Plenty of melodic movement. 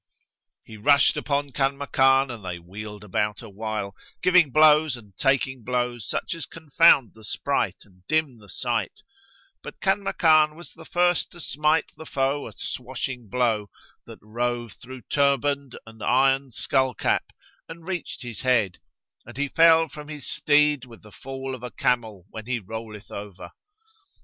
No: average, 4.7 semitones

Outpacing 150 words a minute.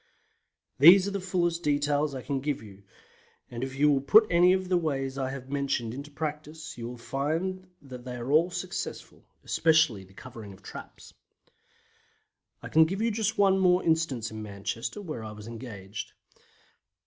Yes: average, 175 wpm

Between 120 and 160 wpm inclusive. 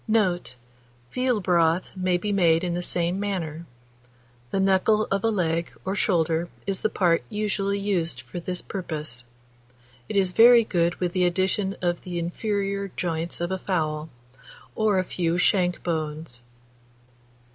Yes: average, 150 wpm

